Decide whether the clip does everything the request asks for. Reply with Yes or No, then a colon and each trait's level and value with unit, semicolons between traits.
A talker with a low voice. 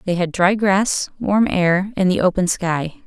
No: medium, 185 Hz